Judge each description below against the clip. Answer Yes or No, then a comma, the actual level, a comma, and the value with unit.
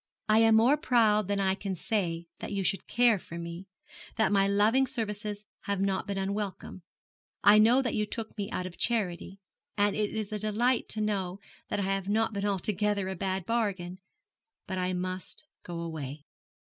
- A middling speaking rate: Yes, average, 185 wpm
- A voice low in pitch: No, high, 200 Hz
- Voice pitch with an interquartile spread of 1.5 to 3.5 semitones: Yes, narrow, 2.4 semitones